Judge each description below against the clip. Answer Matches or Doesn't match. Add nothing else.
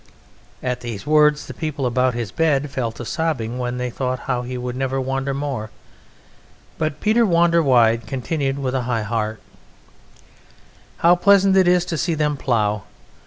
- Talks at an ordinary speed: Matches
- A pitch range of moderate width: Matches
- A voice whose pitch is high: Doesn't match